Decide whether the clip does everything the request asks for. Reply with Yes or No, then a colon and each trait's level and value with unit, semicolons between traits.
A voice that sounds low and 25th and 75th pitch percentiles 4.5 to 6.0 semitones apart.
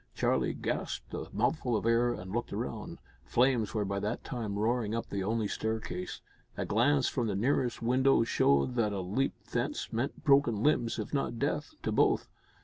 No: low, 115 Hz; average, 3.4 semitones